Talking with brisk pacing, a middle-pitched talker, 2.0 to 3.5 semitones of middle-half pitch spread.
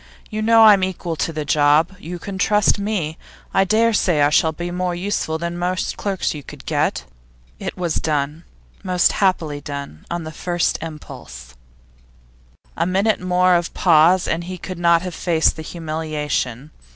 No: average, 175 wpm; medium, 170 Hz; average, 3.0 semitones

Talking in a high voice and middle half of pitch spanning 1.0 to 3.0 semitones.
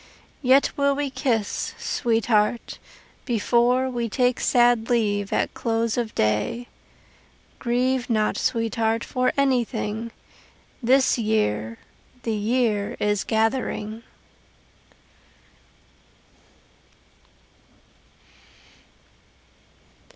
Yes: high, 230 Hz; narrow, 2.6 semitones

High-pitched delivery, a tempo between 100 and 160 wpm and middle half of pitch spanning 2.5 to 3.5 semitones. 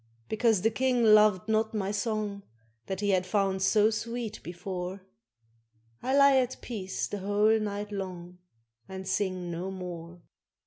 Yes: high, 205 Hz; average, 145 wpm; average, 2.8 semitones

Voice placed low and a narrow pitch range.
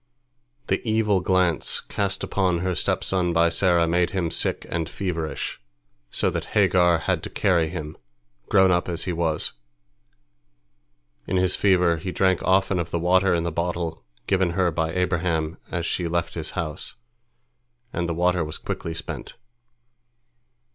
Yes: very low, 85 Hz; narrow, 1.9 semitones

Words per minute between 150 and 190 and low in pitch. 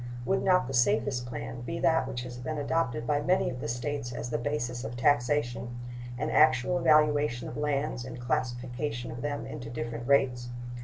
Yes: average, 185 wpm; low, 125 Hz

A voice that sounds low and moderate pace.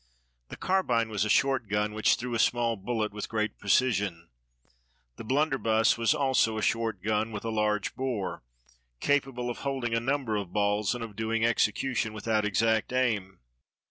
Yes: low, 110 Hz; average, 170 wpm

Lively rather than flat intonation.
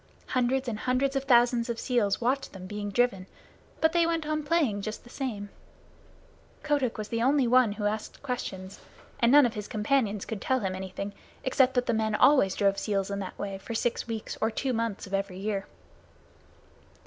No: average, 4.3 semitones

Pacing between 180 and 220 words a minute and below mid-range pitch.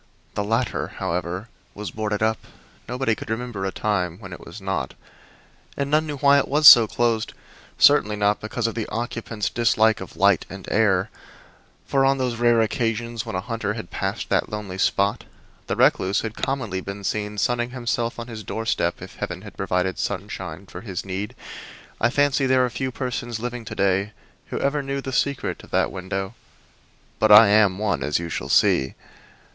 Yes: average, 185 wpm; low, 110 Hz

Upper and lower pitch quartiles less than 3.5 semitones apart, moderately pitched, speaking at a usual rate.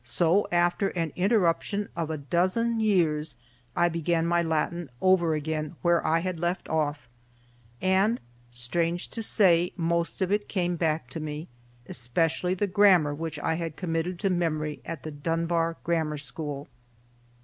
Yes: narrow, 2.5 semitones; medium, 170 Hz; average, 150 wpm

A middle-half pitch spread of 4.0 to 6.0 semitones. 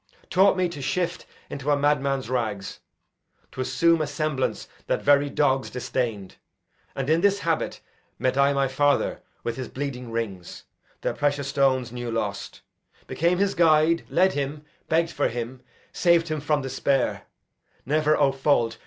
No: average, 3.4 semitones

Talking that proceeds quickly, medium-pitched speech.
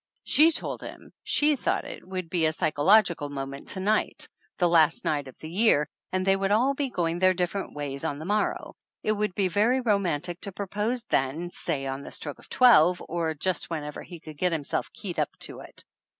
Yes: fast, 210 wpm; medium, 180 Hz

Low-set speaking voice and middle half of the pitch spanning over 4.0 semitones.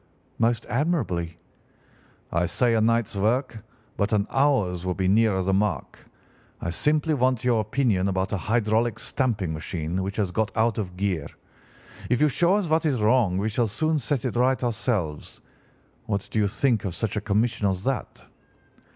Yes: low, 110 Hz; average, 4.6 semitones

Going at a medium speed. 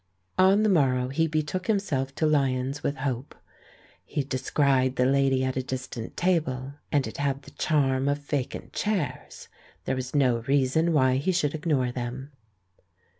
Yes: average, 160 wpm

